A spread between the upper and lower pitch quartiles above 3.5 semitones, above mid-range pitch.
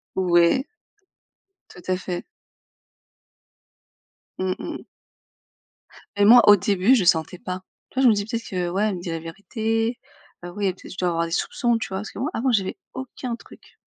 Yes: average, 4.1 semitones; high, 195 Hz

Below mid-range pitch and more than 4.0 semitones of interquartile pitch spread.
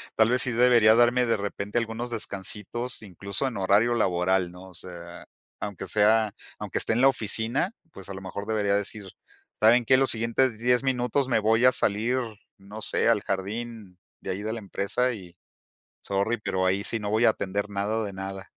No: low, 110 Hz; average, 3.2 semitones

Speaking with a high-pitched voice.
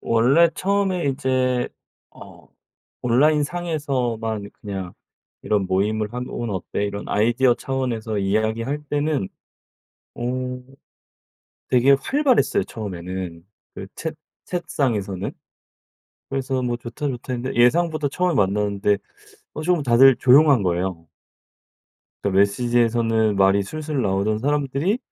No: low, 120 Hz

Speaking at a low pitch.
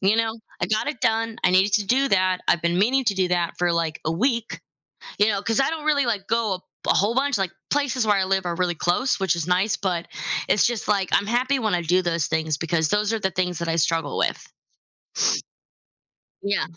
No: high, 195 Hz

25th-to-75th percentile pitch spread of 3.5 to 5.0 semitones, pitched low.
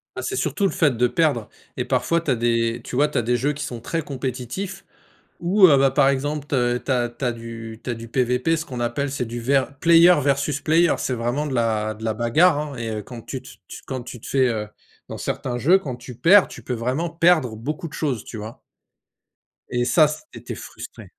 Yes: average, 4.2 semitones; low, 130 Hz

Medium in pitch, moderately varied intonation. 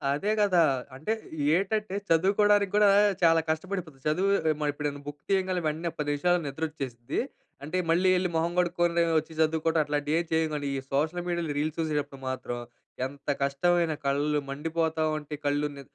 Yes: medium, 160 Hz; average, 3.3 semitones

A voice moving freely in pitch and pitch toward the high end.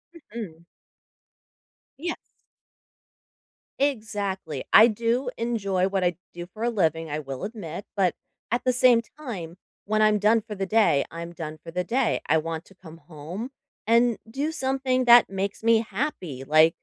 Yes: wide, 5.9 semitones; high, 205 Hz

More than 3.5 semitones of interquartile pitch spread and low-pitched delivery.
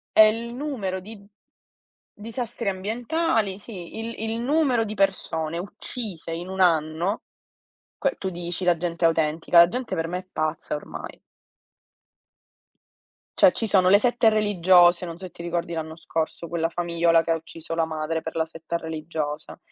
No: average, 4.6 semitones; medium, 175 Hz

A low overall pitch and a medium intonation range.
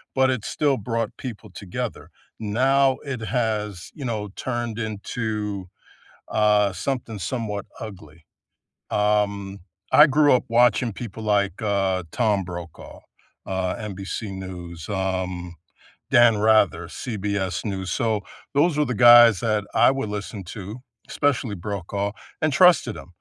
Yes: low, 105 Hz; average, 3.6 semitones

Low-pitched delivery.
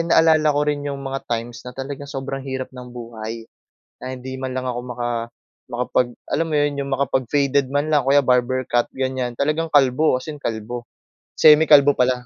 Yes: low, 130 Hz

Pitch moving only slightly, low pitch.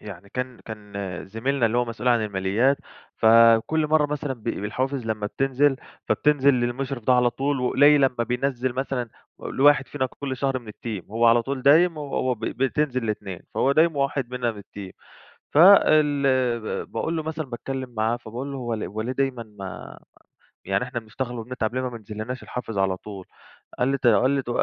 No: average, 3.5 semitones; low, 125 Hz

